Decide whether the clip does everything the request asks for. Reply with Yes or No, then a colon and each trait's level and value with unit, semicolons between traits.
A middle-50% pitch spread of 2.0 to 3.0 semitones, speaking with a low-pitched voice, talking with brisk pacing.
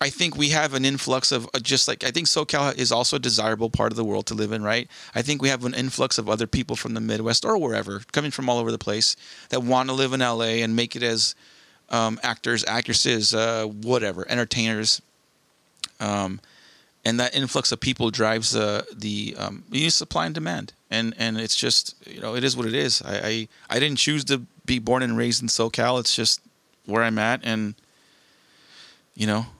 Yes: average, 2.7 semitones; low, 115 Hz; fast, 215 wpm